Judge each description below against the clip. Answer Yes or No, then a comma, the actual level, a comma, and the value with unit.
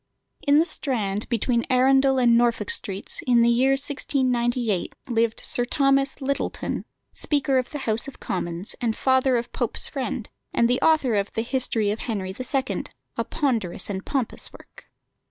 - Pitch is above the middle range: Yes, high, 245 Hz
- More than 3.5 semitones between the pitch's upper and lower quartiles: No, average, 3.2 semitones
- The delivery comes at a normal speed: Yes, average, 165 wpm